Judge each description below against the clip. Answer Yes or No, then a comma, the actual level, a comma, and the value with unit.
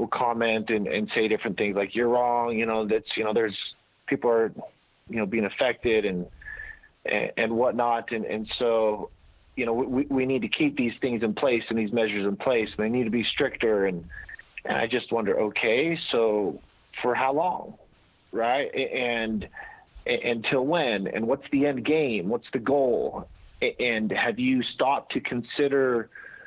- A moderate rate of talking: Yes, average, 175 wpm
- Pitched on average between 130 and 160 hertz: No, low, 120 Hz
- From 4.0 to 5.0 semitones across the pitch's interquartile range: Yes, average, 4.6 semitones